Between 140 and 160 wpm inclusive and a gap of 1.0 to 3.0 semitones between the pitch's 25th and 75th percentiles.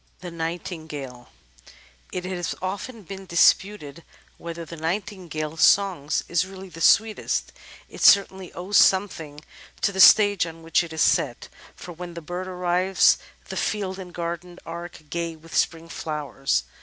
Yes: average, 145 wpm; narrow, 2.6 semitones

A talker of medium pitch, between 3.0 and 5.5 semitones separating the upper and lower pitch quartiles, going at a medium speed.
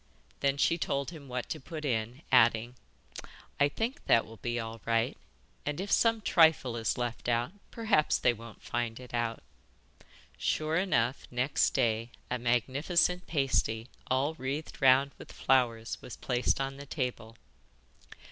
No: low, 130 Hz; average, 4.0 semitones; average, 150 wpm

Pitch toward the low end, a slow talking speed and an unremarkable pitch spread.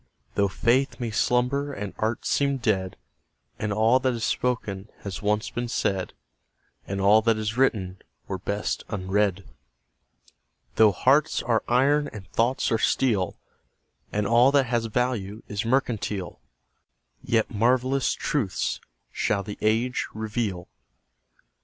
Yes: low, 110 Hz; slow, 130 wpm; average, 3.6 semitones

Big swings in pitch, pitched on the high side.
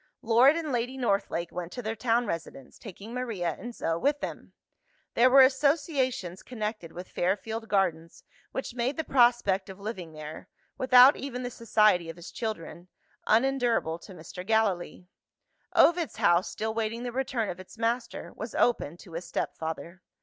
Yes: wide, 5.8 semitones; high, 220 Hz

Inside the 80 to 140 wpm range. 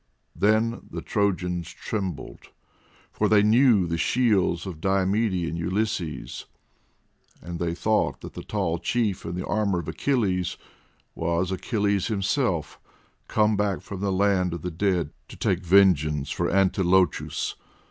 Yes: slow, 135 wpm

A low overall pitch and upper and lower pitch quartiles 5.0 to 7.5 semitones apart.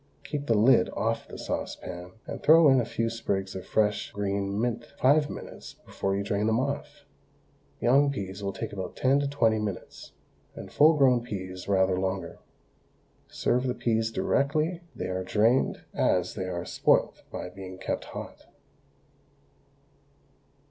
Yes: low, 110 Hz; wide, 5.5 semitones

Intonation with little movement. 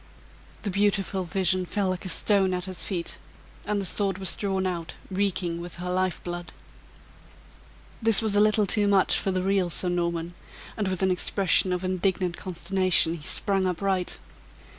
Yes: narrow, 1.9 semitones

